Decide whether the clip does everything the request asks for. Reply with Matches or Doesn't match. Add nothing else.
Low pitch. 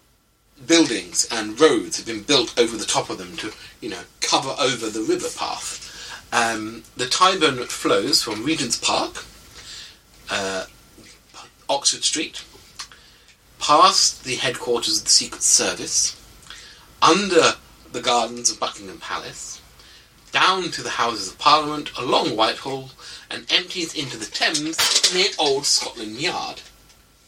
Doesn't match